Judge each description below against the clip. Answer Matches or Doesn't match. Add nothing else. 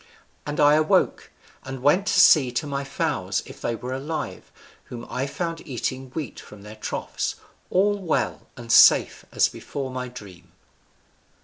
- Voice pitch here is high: Doesn't match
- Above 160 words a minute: Doesn't match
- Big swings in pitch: Doesn't match